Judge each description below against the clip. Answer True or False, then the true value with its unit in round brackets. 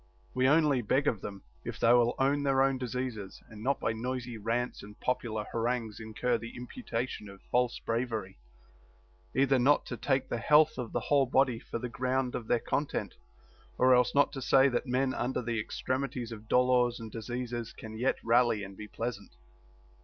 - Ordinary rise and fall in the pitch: False (2.3 semitones)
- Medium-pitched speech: False (125 Hz)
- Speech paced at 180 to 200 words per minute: True (185 wpm)